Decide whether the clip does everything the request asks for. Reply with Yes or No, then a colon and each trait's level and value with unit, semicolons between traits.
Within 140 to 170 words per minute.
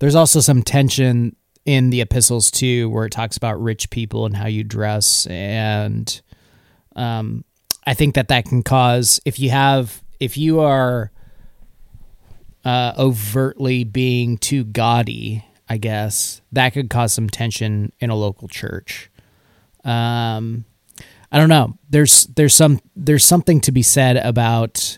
Yes: average, 145 wpm